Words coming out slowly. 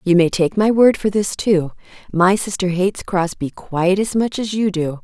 No: fast, 205 wpm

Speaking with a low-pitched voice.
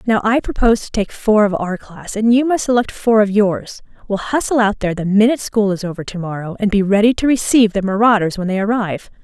No: high, 210 Hz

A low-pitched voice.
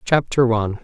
Yes: low, 120 Hz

